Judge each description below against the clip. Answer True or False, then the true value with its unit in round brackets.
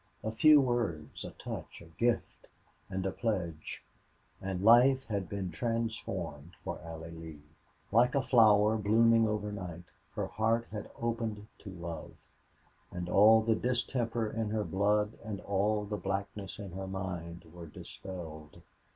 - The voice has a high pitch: False (105 Hz)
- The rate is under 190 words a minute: True (140 wpm)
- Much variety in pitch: False (4.2 semitones)